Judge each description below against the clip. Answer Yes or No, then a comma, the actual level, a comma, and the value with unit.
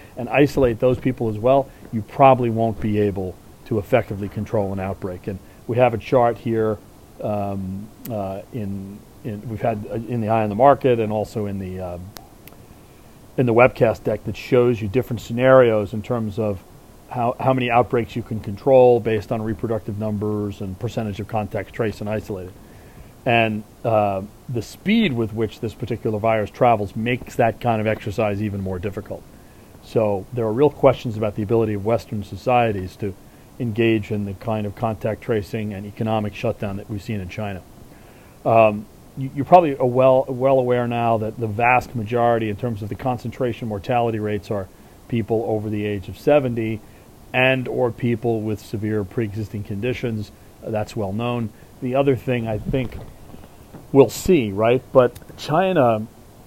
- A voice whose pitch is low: Yes, low, 110 Hz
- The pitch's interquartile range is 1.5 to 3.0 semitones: Yes, narrow, 2.5 semitones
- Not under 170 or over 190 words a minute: Yes, average, 175 wpm